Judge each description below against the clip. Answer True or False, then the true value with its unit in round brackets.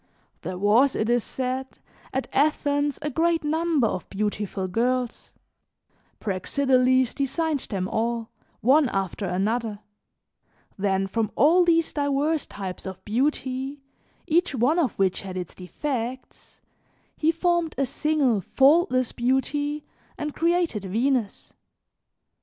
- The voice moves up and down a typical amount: False (5.9 semitones)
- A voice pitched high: True (255 Hz)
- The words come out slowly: True (120 wpm)